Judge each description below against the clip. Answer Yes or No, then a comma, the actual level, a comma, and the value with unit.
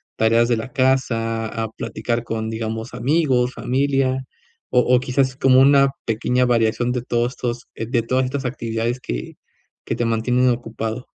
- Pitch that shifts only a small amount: Yes, narrow, 2.3 semitones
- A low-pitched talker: Yes, low, 120 Hz